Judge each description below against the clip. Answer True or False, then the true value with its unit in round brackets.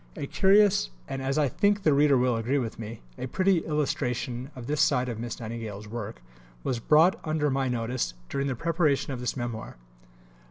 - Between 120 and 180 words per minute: False (190 wpm)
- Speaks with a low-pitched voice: True (130 Hz)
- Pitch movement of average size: True (4.3 semitones)